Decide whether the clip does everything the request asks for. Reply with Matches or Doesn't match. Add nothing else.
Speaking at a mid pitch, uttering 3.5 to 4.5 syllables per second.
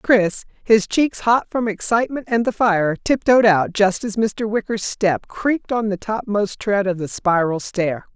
Doesn't match